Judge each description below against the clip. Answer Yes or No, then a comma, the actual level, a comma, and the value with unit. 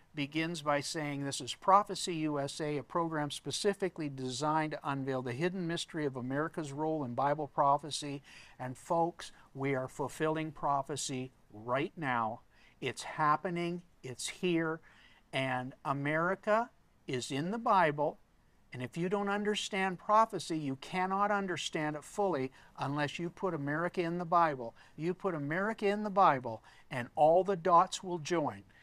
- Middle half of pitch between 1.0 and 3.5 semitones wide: No, average, 4.3 semitones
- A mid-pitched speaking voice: Yes, medium, 155 Hz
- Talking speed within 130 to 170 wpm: Yes, average, 145 wpm